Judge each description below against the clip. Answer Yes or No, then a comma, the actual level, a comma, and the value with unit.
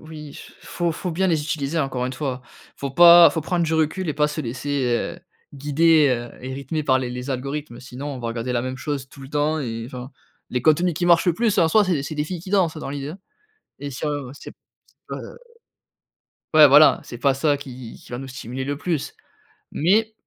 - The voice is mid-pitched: Yes, medium, 145 Hz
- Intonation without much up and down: No, average, 3.6 semitones